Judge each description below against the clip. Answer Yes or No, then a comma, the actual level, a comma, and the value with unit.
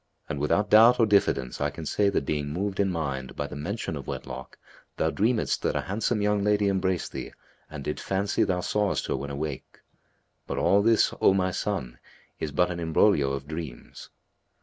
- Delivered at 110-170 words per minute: No, average, 195 wpm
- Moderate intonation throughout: No, wide, 5.9 semitones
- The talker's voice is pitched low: Yes, very low, 90 Hz